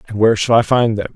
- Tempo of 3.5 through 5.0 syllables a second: No, 7.2 syllables/s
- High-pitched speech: No, low, 110 Hz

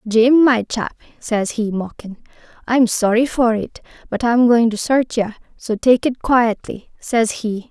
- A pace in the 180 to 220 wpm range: No, average, 170 wpm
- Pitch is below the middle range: No, high, 230 Hz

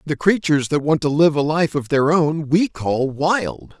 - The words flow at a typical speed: No, fast, 220 wpm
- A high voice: No, medium, 155 Hz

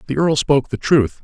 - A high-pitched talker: No, medium, 140 Hz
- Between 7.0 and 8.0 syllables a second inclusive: No, 5.8 syllables/s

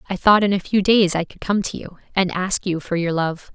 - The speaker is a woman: Yes, female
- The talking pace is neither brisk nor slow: No, fast, 285 wpm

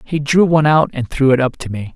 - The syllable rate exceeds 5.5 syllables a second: Yes, 6.0 syllables/s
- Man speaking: Yes, male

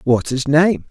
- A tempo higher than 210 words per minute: No, average, 200 wpm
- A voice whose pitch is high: No, medium, 145 Hz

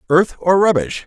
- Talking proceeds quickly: No, average, 170 wpm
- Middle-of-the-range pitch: Yes, medium, 160 Hz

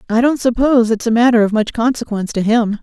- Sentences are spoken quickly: Yes, fast, 235 wpm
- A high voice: Yes, high, 230 Hz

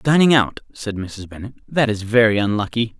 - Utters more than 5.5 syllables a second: No, 5.1 syllables/s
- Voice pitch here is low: Yes, low, 115 Hz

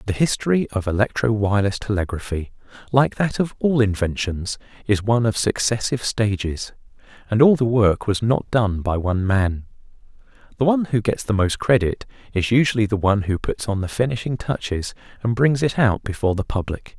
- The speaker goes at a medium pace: Yes, average, 175 wpm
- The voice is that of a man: Yes, male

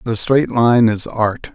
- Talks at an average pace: Yes, average, 195 wpm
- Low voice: Yes, low, 115 Hz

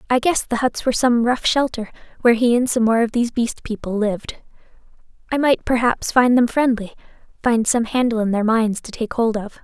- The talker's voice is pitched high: Yes, high, 235 Hz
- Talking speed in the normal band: No, fast, 210 wpm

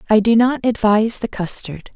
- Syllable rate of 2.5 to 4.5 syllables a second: No, 5.3 syllables/s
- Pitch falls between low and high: No, high, 220 Hz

